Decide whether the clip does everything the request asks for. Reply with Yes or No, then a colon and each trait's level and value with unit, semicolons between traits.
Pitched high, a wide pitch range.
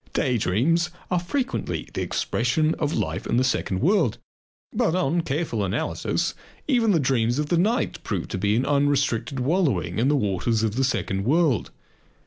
No: low, 135 Hz; wide, 6.9 semitones